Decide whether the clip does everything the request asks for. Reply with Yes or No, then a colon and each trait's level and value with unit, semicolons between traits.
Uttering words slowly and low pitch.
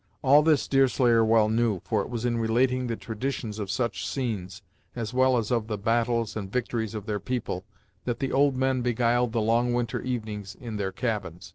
No: average, 200 wpm; low, 115 Hz